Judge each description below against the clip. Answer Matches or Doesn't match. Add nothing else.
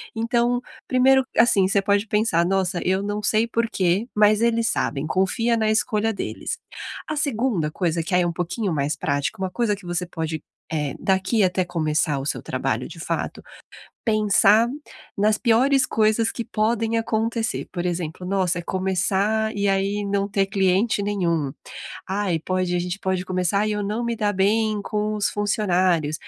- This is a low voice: Doesn't match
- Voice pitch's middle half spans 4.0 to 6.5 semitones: Doesn't match